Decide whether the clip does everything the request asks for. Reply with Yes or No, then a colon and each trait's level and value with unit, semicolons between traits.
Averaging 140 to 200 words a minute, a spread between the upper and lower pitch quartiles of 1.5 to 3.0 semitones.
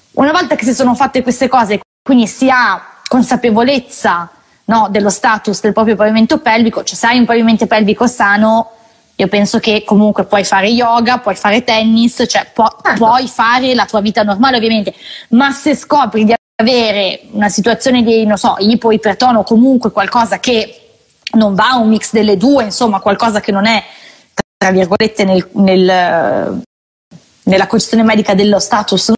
Yes: average, 165 wpm; average, 2.7 semitones